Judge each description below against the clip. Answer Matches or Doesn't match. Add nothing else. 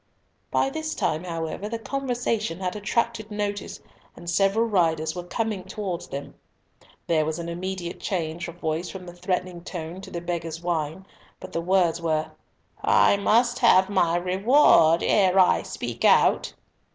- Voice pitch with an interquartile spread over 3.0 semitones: Matches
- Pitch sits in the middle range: Matches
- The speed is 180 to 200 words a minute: Doesn't match